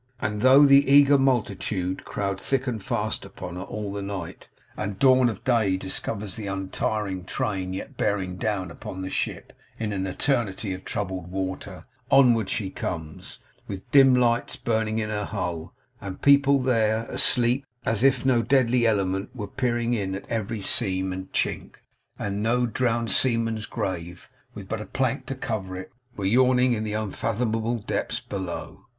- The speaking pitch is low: Yes, low, 110 Hz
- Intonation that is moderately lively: Yes, average, 4.1 semitones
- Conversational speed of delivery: Yes, average, 165 wpm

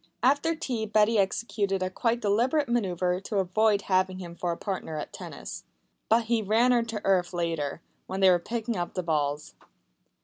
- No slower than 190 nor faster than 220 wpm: No, average, 180 wpm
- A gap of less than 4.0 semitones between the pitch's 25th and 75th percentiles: No, average, 4.3 semitones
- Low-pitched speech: No, high, 200 Hz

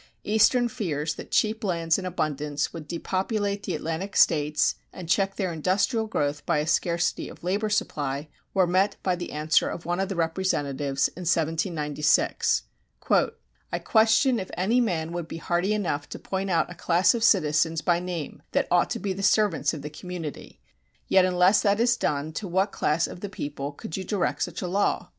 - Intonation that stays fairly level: No, average, 4.0 semitones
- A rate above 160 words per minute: Yes, average, 190 wpm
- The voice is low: No, medium, 175 Hz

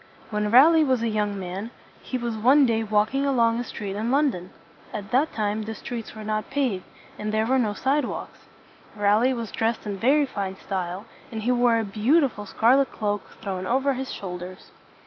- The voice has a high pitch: Yes, high, 225 Hz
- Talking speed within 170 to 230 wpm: Yes, average, 200 wpm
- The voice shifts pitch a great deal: No, average, 3.8 semitones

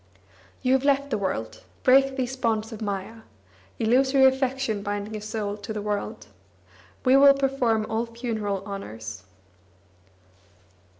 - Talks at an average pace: No, slow, 130 wpm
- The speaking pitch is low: No, high, 225 Hz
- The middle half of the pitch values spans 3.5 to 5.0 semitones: Yes, average, 4.4 semitones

